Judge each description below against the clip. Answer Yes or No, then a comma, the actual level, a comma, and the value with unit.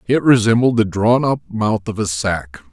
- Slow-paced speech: No, average, 200 wpm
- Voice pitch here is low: Yes, low, 110 Hz